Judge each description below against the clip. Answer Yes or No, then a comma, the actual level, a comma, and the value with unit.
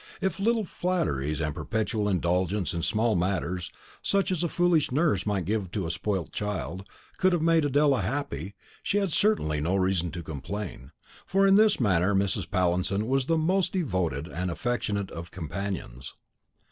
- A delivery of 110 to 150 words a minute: No, average, 170 wpm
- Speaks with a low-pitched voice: Yes, low, 100 Hz